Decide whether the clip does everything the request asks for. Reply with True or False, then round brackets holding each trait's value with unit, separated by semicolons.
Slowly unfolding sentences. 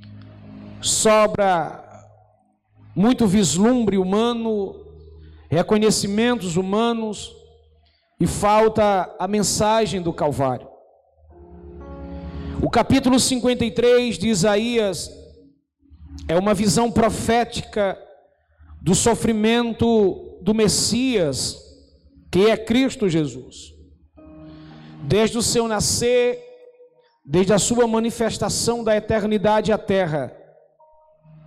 True (80 wpm)